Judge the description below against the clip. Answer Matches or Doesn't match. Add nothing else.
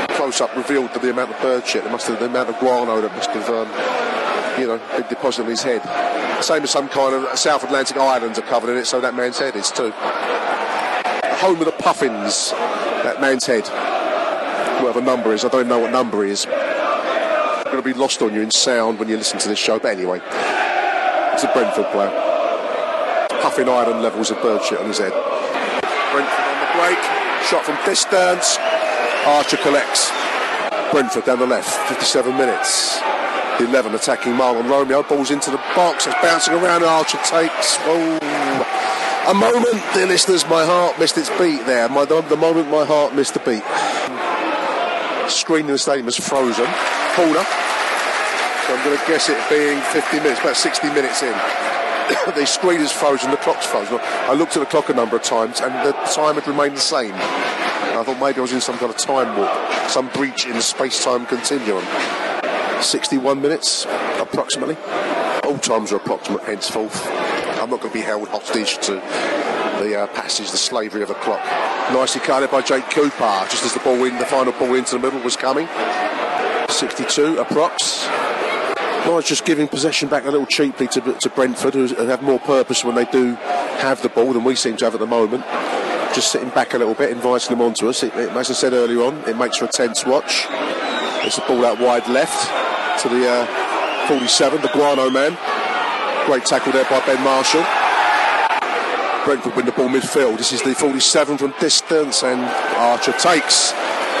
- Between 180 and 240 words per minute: Matches